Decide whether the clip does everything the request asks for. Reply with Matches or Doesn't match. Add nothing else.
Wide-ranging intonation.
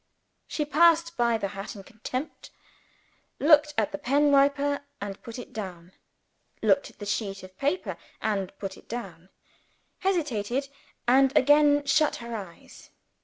Matches